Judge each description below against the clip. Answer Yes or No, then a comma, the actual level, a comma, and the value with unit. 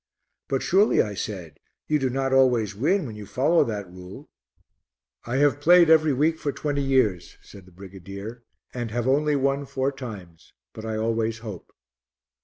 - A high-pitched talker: No, low, 125 Hz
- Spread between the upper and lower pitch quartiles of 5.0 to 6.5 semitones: Yes, average, 5.3 semitones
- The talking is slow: No, average, 170 wpm